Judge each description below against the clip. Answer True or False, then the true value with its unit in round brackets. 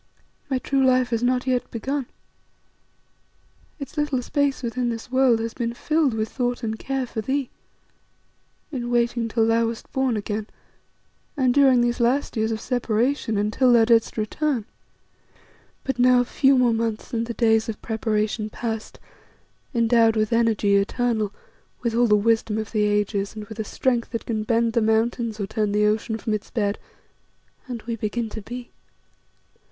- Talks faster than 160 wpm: True (170 wpm)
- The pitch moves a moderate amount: False (2.2 semitones)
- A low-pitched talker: False (230 Hz)